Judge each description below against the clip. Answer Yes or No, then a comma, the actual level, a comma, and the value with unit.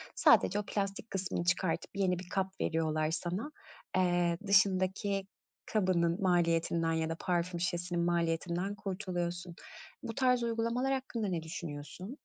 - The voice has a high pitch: No, medium, 180 Hz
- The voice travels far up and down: No, narrow, 2.6 semitones